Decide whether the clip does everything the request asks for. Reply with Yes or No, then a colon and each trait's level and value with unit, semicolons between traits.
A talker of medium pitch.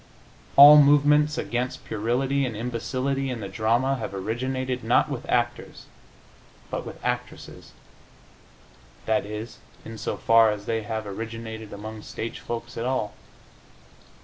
No: low, 115 Hz